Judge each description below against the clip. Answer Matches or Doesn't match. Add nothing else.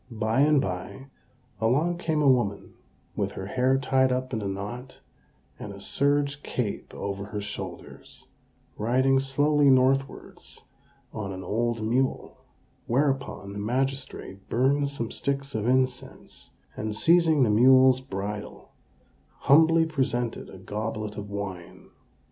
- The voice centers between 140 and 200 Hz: Doesn't match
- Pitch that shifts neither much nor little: Matches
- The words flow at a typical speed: Doesn't match